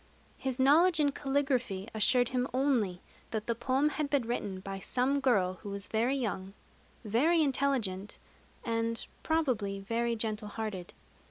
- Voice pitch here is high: Yes, high, 235 Hz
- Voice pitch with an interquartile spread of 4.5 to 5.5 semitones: Yes, average, 4.9 semitones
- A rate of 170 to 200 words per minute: No, average, 145 wpm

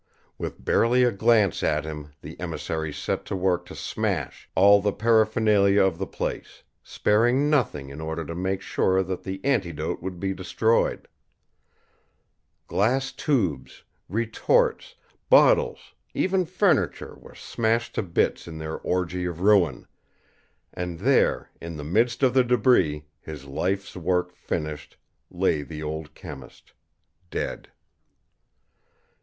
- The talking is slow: Yes, slow, 130 wpm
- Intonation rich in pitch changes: Yes, wide, 6.0 semitones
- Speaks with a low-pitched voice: Yes, very low, 95 Hz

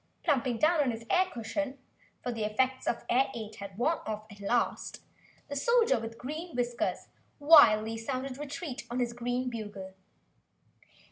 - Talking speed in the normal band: Yes, average, 160 wpm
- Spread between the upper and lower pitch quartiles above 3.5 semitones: Yes, average, 4.0 semitones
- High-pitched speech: Yes, high, 245 Hz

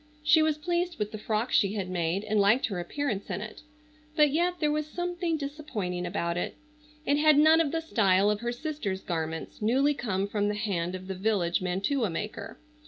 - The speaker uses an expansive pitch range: Yes, wide, 7.8 semitones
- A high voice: Yes, high, 215 Hz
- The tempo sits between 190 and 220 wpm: Yes, average, 200 wpm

